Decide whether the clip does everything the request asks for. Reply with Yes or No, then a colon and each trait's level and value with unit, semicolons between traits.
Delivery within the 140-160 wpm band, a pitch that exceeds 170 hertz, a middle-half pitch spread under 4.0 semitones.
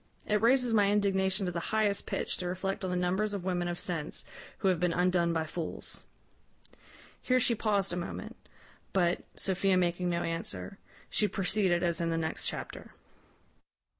No: average, 170 wpm; medium, 185 Hz; average, 2.7 semitones